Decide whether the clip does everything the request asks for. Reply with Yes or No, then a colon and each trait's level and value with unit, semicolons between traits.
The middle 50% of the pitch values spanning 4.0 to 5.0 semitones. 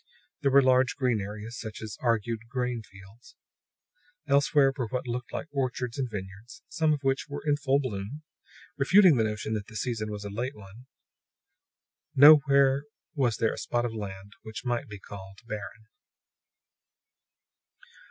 Yes: average, 4.3 semitones